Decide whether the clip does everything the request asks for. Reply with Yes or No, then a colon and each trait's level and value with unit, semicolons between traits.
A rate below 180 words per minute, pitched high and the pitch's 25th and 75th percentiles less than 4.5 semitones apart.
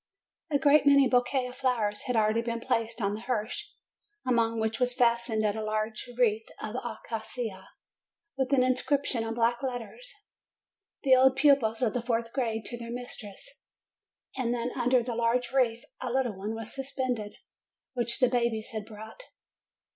Yes: average, 160 wpm; high, 235 Hz; narrow, 2.4 semitones